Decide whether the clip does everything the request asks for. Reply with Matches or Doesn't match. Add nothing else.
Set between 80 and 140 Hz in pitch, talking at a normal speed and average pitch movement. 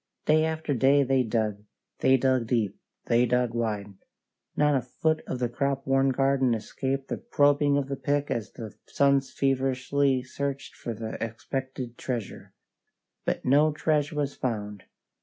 Matches